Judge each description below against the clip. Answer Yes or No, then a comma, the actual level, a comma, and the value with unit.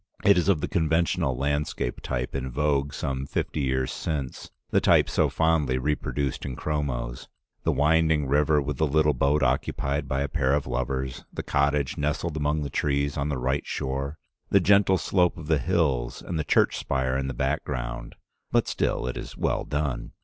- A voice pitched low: Yes, very low, 70 Hz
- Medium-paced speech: Yes, average, 185 wpm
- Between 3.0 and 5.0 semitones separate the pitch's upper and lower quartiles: No, narrow, 2.6 semitones